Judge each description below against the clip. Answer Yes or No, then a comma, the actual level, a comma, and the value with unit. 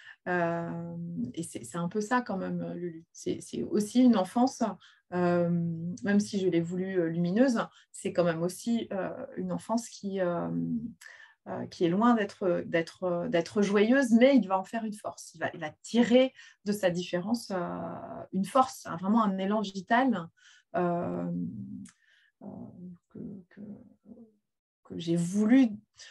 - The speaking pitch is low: No, high, 195 Hz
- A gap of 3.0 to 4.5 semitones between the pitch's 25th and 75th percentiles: No, average, 5.0 semitones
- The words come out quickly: No, average, 155 wpm